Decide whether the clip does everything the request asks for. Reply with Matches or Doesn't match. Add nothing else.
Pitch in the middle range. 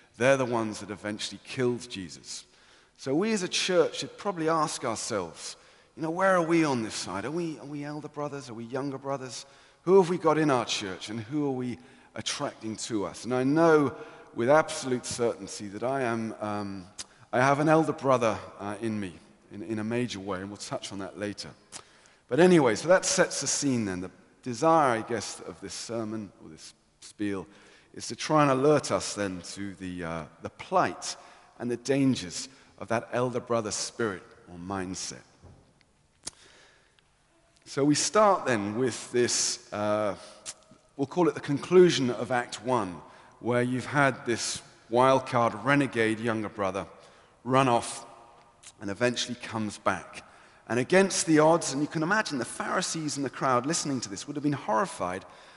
Doesn't match